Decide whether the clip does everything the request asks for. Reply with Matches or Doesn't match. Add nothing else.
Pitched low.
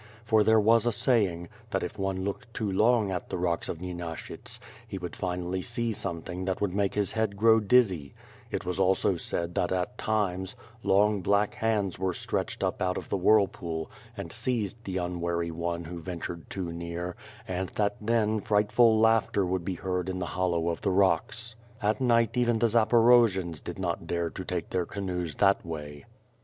Matches